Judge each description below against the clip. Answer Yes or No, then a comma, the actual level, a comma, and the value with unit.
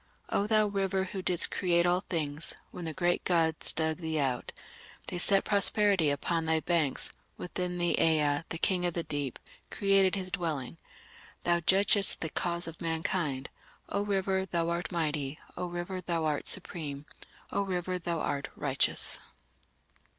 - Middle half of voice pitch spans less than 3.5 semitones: Yes, average, 2.9 semitones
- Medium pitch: Yes, medium, 170 Hz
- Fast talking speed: No, average, 160 wpm